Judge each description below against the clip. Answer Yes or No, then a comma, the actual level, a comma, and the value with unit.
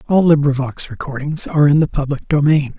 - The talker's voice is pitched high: No, medium, 145 Hz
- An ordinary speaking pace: Yes, average, 170 wpm